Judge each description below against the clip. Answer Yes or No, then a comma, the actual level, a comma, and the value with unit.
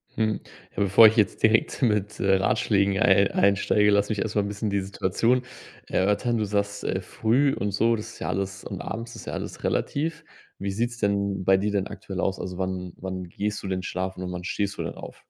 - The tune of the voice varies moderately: No, narrow, 2.3 semitones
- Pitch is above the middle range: No, low, 100 Hz